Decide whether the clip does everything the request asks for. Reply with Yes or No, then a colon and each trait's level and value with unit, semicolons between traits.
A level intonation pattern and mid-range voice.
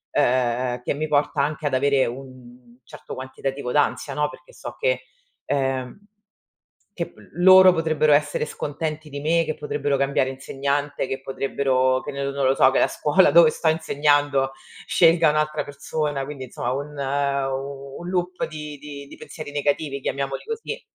Yes: narrow, 2.2 semitones; medium, 145 Hz